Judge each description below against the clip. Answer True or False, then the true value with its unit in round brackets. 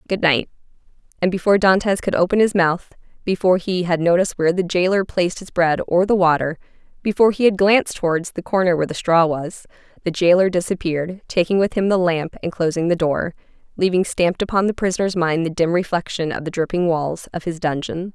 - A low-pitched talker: False (175 Hz)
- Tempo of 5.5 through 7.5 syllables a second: True (6.1 syllables/s)